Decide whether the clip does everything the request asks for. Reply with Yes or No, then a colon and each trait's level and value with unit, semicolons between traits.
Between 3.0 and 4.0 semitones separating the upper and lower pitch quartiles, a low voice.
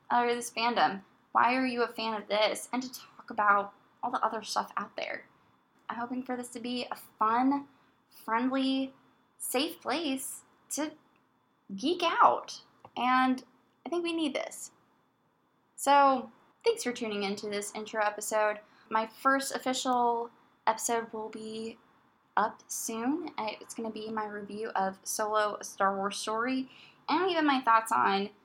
No: average, 3.6 semitones; high, 235 Hz